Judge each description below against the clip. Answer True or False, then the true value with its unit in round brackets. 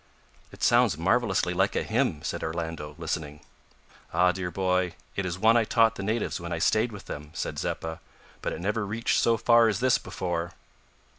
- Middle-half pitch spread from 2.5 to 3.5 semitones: False (4.9 semitones)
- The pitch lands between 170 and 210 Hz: False (95 Hz)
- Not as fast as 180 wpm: False (190 wpm)